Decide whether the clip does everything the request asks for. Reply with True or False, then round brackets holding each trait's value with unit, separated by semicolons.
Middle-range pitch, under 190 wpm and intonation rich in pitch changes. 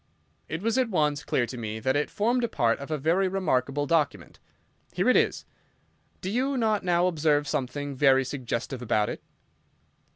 True (150 Hz; 170 wpm; 6.2 semitones)